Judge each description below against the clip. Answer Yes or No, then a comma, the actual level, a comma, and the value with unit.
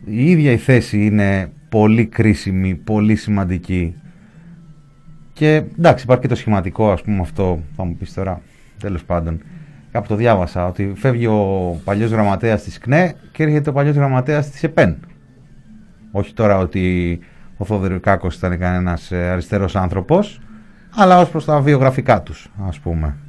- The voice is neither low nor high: No, low, 105 Hz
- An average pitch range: No, wide, 7.6 semitones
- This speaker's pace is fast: No, average, 150 wpm